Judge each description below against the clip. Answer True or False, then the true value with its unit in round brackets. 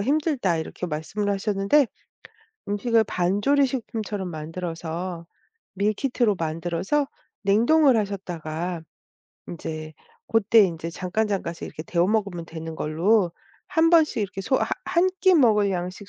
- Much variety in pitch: False (4.9 semitones)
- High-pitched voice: True (195 Hz)